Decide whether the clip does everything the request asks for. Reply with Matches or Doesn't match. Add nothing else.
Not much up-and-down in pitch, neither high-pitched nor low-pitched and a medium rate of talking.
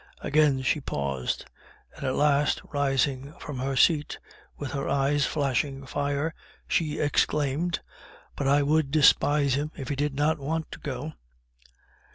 Matches